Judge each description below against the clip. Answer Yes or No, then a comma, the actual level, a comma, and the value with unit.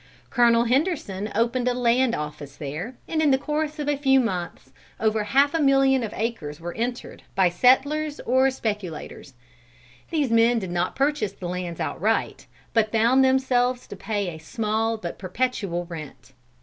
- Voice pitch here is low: No, high, 230 Hz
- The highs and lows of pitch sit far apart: Yes, wide, 6.1 semitones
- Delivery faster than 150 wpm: Yes, average, 160 wpm